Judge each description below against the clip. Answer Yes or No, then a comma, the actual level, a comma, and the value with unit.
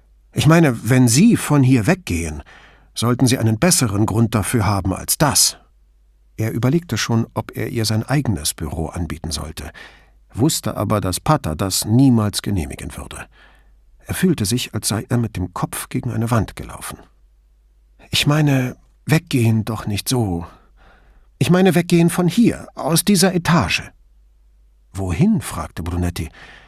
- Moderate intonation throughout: No, wide, 8.1 semitones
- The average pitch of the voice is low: Yes, low, 110 Hz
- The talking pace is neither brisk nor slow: Yes, average, 145 wpm